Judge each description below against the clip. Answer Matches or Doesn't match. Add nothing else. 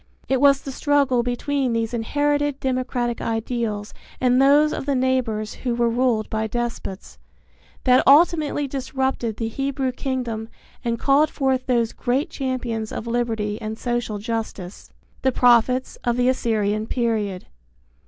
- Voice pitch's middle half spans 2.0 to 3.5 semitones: Matches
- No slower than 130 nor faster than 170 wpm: Matches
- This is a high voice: Matches